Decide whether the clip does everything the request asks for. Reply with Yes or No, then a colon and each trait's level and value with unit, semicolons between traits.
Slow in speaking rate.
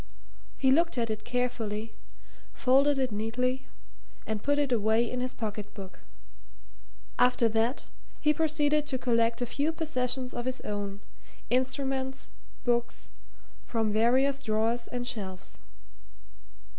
Yes: slow, 125 wpm